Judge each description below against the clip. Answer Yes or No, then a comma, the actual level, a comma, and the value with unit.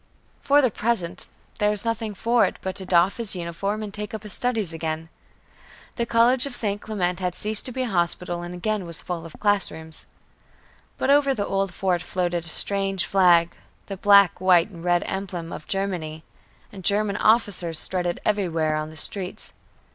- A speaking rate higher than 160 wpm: Yes, average, 185 wpm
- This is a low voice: No, high, 190 Hz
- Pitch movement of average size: Yes, average, 3.5 semitones